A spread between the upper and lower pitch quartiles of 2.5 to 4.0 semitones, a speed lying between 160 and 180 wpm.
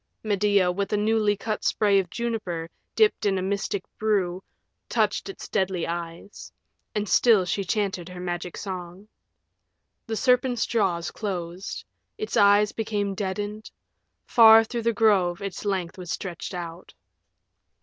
No: average, 3.1 semitones; average, 140 wpm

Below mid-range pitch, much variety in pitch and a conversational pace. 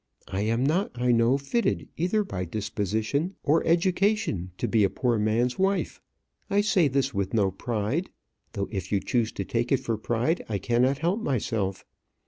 Yes: low, 120 Hz; wide, 7.4 semitones; average, 175 wpm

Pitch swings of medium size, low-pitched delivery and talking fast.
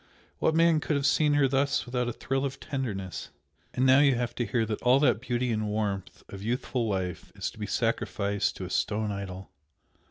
Yes: average, 4.7 semitones; low, 120 Hz; fast, 210 wpm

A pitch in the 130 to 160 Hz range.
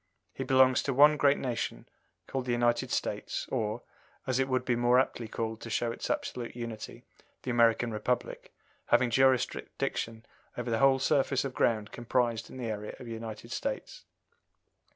No: low, 120 Hz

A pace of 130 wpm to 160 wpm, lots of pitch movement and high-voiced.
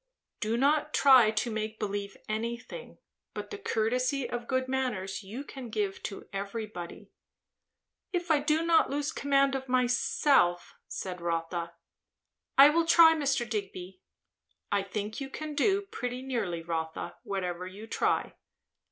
Yes: average, 140 wpm; wide, 5.9 semitones; high, 235 Hz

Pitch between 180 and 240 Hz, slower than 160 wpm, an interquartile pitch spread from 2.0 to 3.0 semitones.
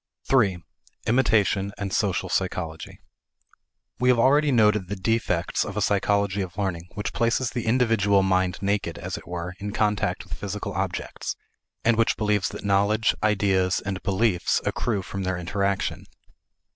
No: low, 100 Hz; average, 150 wpm; narrow, 2.6 semitones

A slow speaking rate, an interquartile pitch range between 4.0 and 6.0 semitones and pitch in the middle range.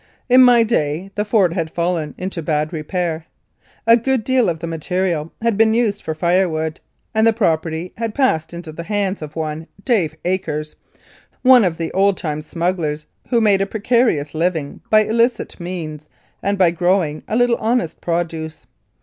No: average, 170 wpm; average, 5.3 semitones; medium, 180 Hz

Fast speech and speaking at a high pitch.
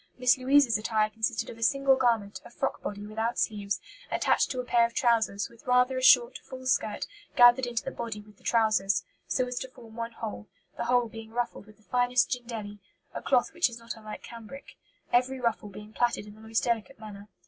Yes: fast, 215 wpm; high, 235 Hz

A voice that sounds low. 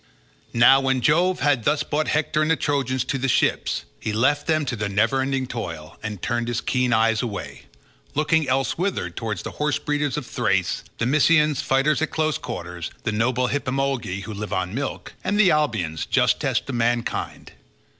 Yes: low, 130 Hz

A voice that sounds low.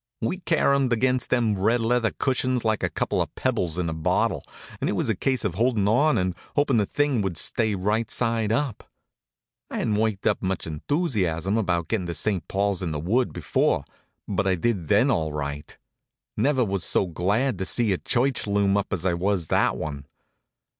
Yes: low, 105 Hz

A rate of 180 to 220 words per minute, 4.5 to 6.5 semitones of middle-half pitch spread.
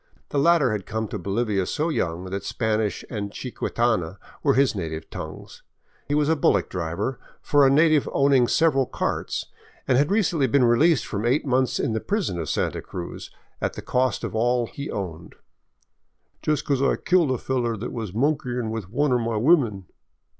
Yes: average, 185 wpm; average, 5.3 semitones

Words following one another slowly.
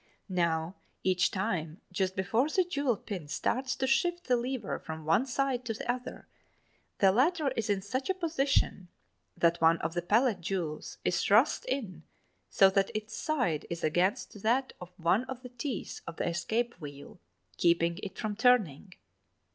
No: average, 170 wpm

